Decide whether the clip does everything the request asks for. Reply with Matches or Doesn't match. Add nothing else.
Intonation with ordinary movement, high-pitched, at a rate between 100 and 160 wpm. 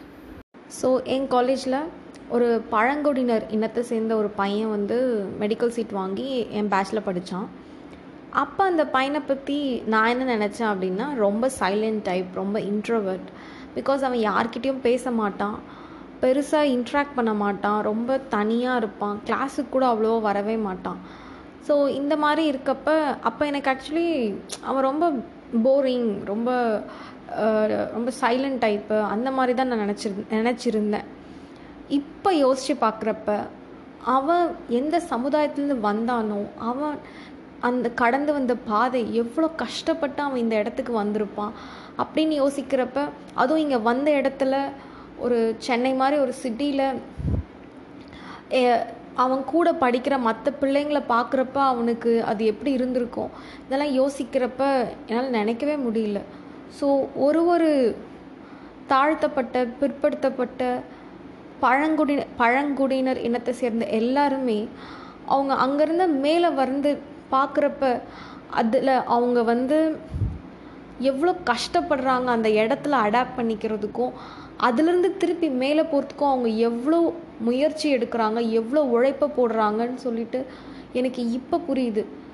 Matches